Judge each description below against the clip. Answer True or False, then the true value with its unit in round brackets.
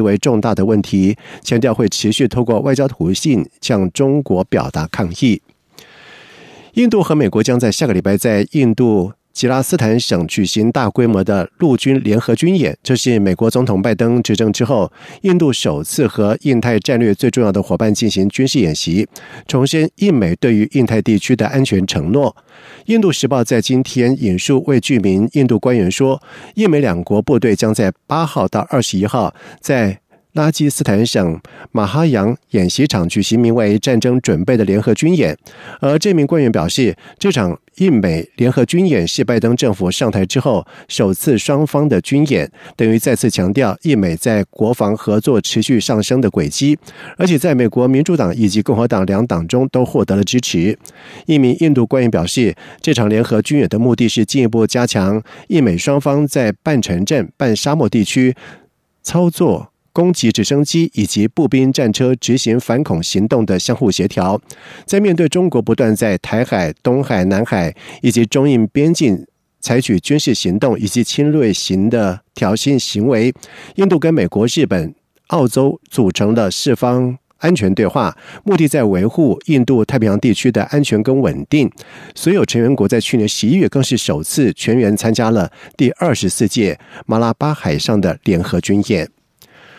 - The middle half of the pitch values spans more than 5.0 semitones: False (4.7 semitones)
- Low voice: True (120 Hz)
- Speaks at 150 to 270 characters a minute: True (265 characters per minute)